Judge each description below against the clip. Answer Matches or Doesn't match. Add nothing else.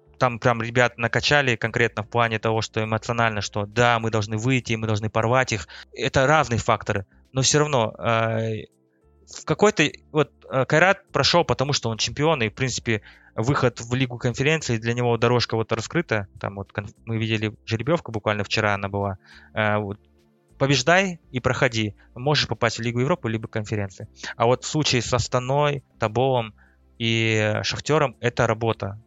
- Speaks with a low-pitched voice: Matches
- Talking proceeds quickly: Matches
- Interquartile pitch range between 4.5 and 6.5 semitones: Doesn't match